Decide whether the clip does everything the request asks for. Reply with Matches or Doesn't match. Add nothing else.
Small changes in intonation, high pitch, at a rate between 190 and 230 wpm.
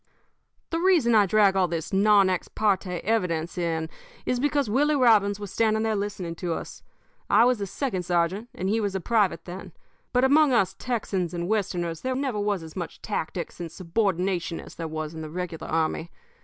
Doesn't match